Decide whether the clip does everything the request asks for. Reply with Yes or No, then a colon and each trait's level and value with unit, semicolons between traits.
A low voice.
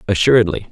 Yes: low, 105 Hz